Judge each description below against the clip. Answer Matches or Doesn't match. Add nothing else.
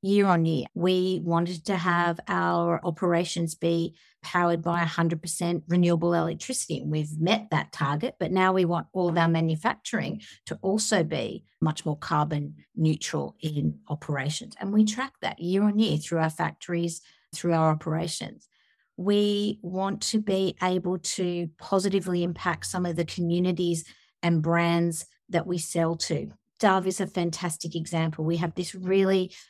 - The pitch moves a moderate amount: Doesn't match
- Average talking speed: Matches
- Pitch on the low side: Doesn't match